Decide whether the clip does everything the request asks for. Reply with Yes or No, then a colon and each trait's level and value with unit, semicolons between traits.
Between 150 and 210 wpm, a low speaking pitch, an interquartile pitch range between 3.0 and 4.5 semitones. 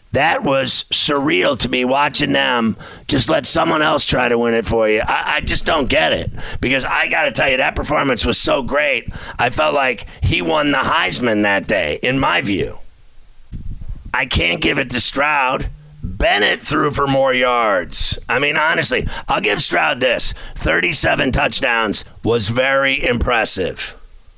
Yes: average, 170 wpm; low, 125 Hz; average, 3.8 semitones